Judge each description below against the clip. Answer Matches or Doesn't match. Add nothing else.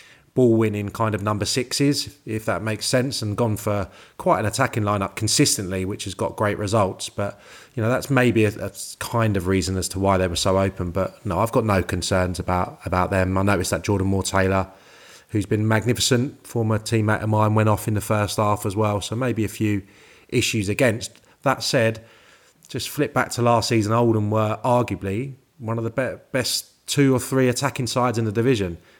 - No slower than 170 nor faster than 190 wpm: Doesn't match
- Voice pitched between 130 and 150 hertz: Doesn't match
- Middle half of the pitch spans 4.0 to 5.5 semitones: Doesn't match